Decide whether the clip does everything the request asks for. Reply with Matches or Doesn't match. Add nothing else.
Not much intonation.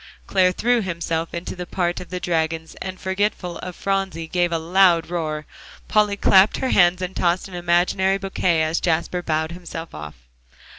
Matches